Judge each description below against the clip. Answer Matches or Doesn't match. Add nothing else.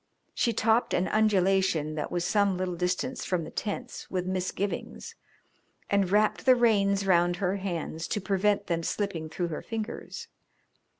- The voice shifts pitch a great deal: Doesn't match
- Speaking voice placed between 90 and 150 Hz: Doesn't match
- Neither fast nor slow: Matches